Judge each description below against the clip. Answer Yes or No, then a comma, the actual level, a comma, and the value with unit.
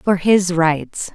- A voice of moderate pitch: Yes, medium, 180 Hz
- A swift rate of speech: No, average, 155 wpm